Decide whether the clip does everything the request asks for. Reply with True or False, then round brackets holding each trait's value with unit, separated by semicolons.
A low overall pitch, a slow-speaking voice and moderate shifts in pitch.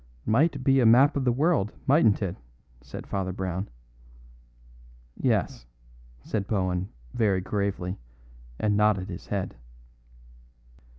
True (100 Hz; 115 wpm; 4.8 semitones)